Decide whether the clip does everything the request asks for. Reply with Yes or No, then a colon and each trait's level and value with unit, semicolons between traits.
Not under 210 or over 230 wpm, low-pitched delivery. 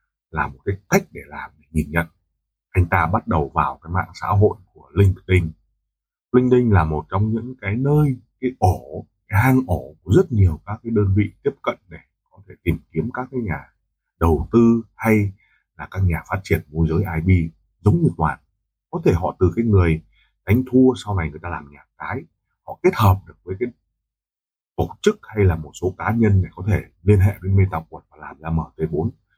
Yes: average, 215 wpm; very low, 95 Hz